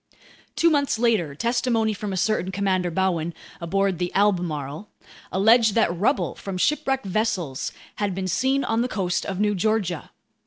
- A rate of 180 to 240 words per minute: No, average, 155 wpm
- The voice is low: No, high, 195 Hz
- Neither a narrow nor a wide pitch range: Yes, average, 4.0 semitones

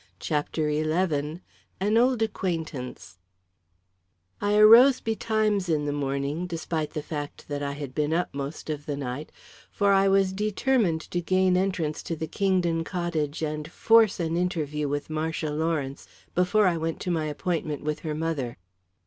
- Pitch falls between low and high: Yes, medium, 160 Hz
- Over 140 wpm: Yes, average, 155 wpm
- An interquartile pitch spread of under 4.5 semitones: Yes, average, 4.0 semitones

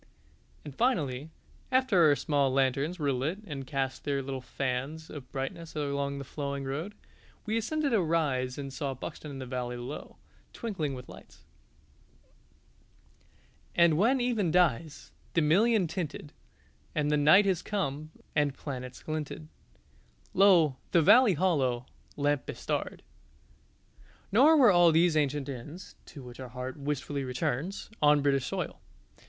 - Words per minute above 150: No, average, 140 wpm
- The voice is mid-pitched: Yes, medium, 150 Hz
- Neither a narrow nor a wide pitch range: Yes, average, 4.5 semitones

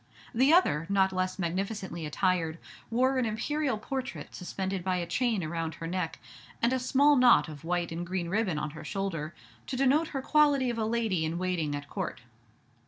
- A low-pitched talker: No, high, 190 Hz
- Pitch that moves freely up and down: Yes, wide, 6.9 semitones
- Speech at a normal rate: Yes, average, 185 wpm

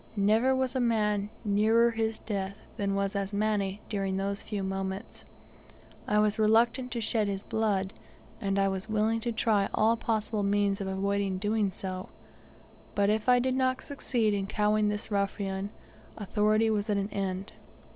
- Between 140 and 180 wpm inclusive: Yes, average, 165 wpm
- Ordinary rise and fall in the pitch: No, narrow, 2.0 semitones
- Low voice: No, high, 210 Hz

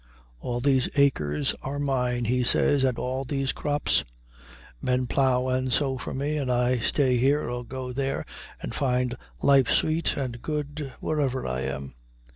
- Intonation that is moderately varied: No, narrow, 2.2 semitones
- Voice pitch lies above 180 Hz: No, low, 130 Hz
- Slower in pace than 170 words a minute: Yes, average, 160 wpm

